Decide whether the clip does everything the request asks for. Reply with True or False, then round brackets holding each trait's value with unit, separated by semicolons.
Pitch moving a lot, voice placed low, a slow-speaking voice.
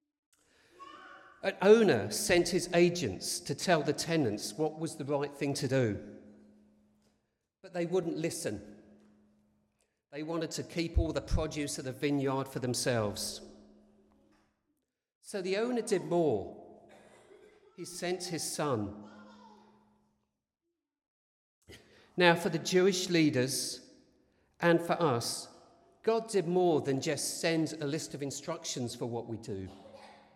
False (6.3 semitones; 155 Hz; 125 wpm)